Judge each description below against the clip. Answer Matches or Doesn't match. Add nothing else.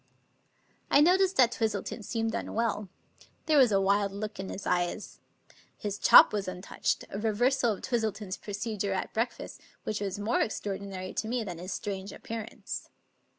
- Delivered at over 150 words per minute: Matches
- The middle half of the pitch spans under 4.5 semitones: Matches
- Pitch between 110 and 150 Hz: Doesn't match